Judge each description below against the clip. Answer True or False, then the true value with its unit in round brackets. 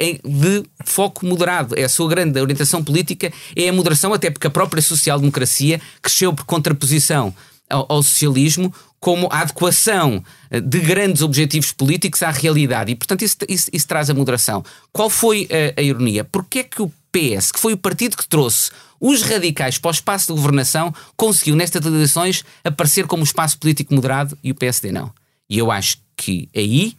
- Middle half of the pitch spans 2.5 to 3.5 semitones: False (4.4 semitones)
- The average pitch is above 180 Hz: False (155 Hz)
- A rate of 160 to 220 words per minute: True (180 wpm)